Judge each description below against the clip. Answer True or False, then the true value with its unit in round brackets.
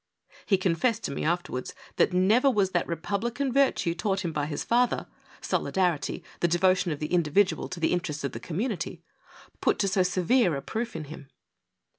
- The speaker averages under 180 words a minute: False (190 wpm)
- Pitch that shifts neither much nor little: True (4.3 semitones)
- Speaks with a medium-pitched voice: True (180 Hz)